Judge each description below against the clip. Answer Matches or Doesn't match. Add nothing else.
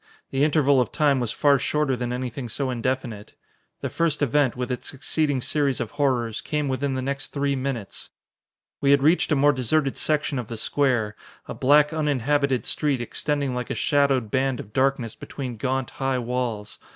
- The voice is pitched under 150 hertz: Matches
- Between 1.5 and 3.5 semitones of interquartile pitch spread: Matches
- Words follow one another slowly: Doesn't match